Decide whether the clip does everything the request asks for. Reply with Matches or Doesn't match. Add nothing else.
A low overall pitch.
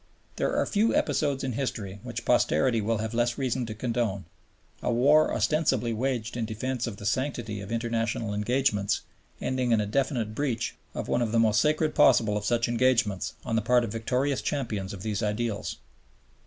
Matches